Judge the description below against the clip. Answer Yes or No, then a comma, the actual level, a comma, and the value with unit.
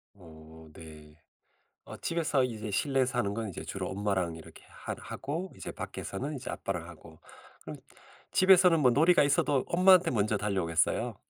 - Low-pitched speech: Yes, low, 110 Hz